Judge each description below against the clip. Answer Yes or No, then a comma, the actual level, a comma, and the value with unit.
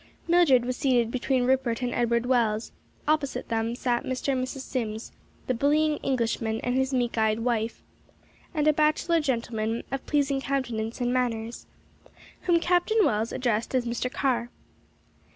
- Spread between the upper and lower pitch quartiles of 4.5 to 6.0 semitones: No, average, 2.9 semitones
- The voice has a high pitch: Yes, very high, 250 Hz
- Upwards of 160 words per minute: No, average, 150 wpm